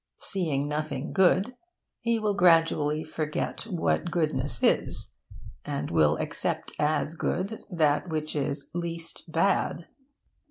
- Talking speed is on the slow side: Yes, slow, 115 wpm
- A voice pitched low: No, medium, 160 Hz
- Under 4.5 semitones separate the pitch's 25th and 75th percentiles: Yes, average, 3.1 semitones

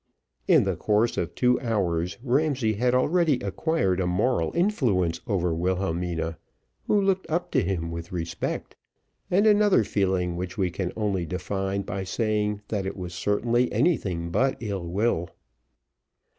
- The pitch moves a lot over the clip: Yes, wide, 5.8 semitones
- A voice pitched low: Yes, low, 100 Hz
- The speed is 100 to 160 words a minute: Yes, average, 145 wpm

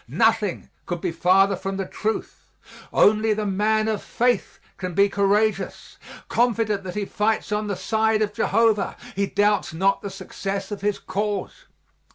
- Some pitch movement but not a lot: No, narrow, 1.9 semitones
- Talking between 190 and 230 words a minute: No, average, 160 wpm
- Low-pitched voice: No, high, 205 Hz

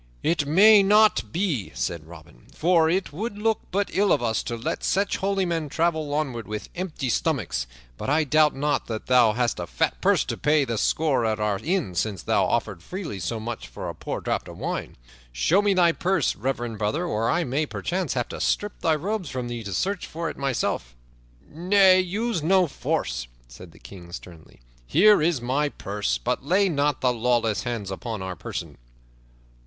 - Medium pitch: Yes, medium, 145 Hz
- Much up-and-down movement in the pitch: Yes, wide, 8.2 semitones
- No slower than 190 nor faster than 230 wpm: Yes, average, 195 wpm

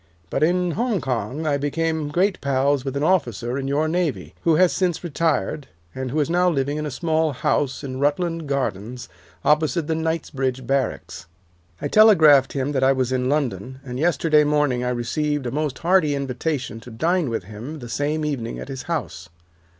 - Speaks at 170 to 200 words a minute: Yes, average, 190 wpm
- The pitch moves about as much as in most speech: Yes, average, 3.7 semitones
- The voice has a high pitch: No, medium, 145 Hz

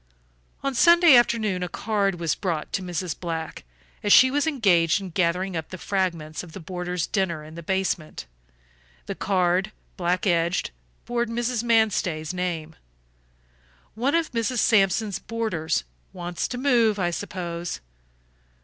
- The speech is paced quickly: No, average, 140 wpm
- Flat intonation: No, average, 4.8 semitones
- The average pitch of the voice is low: No, medium, 185 Hz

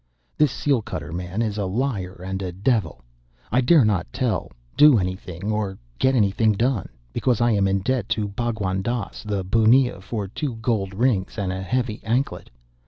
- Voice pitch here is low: Yes, low, 105 Hz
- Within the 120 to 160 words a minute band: No, average, 175 wpm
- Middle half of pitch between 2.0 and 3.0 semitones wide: No, average, 4.1 semitones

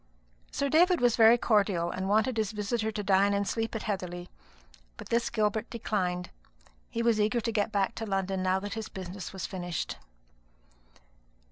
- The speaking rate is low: No, average, 170 wpm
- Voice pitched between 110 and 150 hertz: No, high, 210 Hz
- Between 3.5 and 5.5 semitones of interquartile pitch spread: No, average, 3.0 semitones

